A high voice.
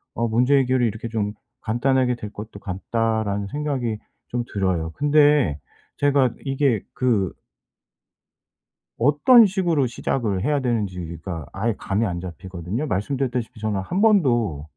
No: low, 115 Hz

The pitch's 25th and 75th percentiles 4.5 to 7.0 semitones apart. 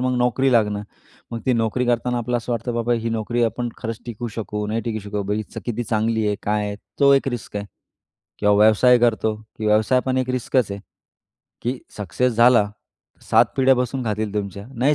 No: average, 2.7 semitones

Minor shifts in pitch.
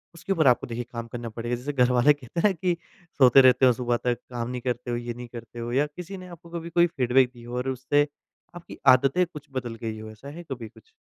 No: average, 3.7 semitones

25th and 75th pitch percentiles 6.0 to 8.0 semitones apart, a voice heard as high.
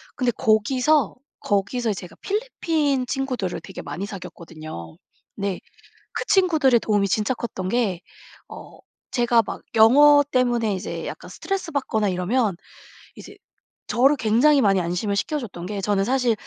No: average, 5.3 semitones; high, 230 Hz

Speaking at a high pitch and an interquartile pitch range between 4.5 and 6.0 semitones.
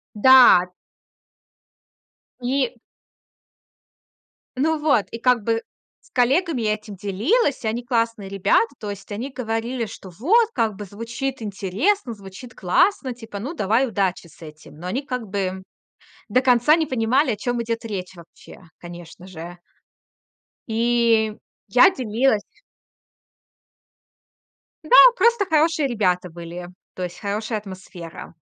Yes: high, 225 Hz; average, 4.9 semitones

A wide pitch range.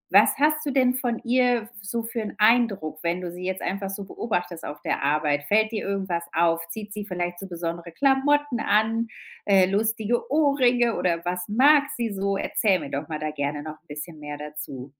Yes: wide, 5.8 semitones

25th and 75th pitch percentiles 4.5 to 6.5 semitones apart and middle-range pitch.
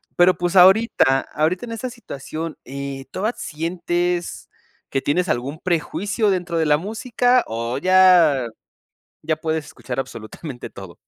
Yes: average, 5.2 semitones; medium, 170 Hz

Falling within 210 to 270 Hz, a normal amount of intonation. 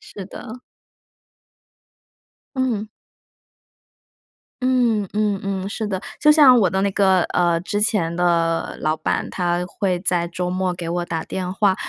No: high, 190 Hz; average, 3.1 semitones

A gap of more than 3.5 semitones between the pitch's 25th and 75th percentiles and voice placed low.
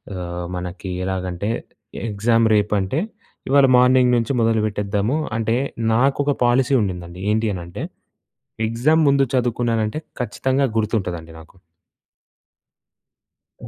Yes: average, 4.8 semitones; low, 110 Hz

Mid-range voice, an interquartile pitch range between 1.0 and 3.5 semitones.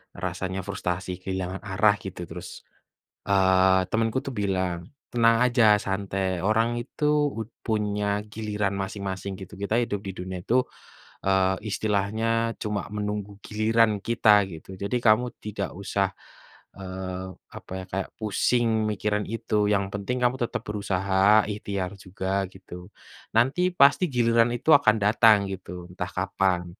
No: low, 100 Hz; average, 2.7 semitones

